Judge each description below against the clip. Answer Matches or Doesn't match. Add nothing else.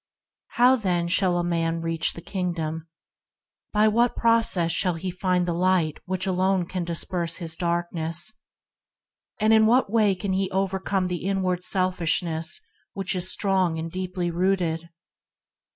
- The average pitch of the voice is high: Doesn't match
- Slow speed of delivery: Doesn't match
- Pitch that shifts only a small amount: Matches